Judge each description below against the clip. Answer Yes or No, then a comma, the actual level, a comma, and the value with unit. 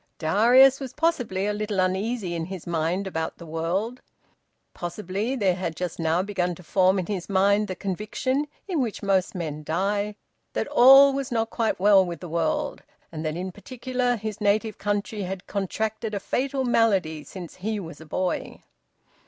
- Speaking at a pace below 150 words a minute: No, average, 175 wpm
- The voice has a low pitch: No, high, 200 Hz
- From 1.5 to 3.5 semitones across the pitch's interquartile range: No, average, 4.1 semitones